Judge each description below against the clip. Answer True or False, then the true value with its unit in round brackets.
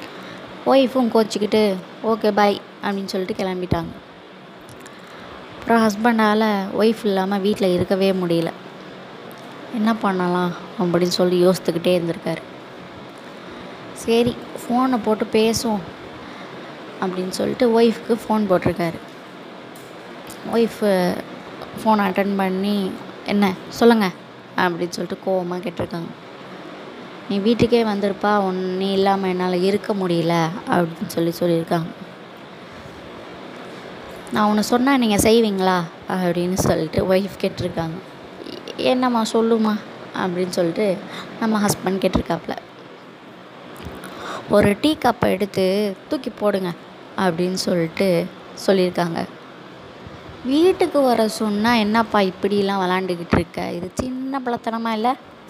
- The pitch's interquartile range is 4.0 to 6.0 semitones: False (3.5 semitones)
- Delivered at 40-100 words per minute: True (90 wpm)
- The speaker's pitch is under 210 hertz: True (200 Hz)